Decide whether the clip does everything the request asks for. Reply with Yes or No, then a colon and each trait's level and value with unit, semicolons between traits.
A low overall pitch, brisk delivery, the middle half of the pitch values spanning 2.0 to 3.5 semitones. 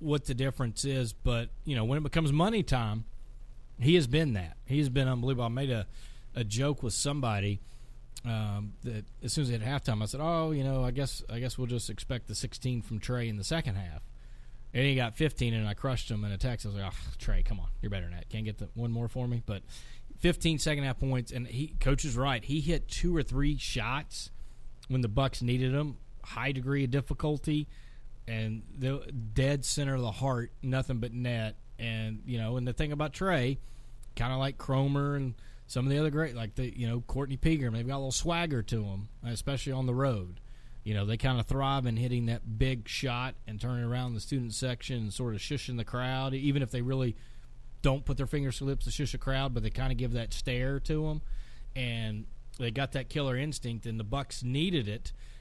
Yes: low, 125 Hz; fast, 230 wpm; average, 2.9 semitones